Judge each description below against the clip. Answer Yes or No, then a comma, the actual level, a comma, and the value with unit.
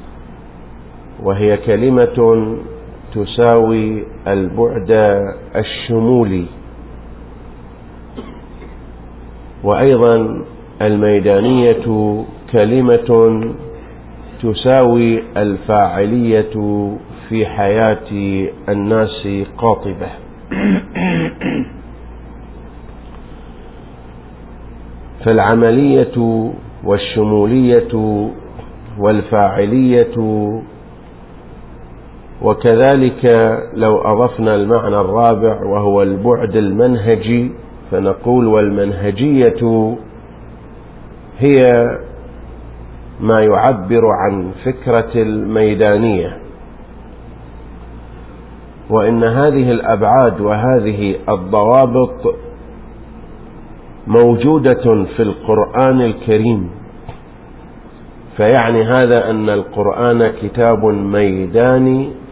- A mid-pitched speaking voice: No, low, 110 Hz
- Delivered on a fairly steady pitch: No, average, 3.1 semitones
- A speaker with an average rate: No, slow, 45 wpm